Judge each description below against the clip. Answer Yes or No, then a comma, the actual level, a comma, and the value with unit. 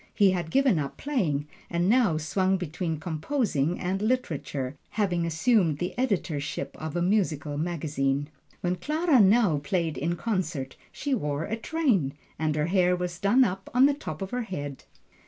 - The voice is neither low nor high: Yes, medium, 180 Hz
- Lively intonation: Yes, wide, 5.8 semitones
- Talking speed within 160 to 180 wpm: Yes, average, 165 wpm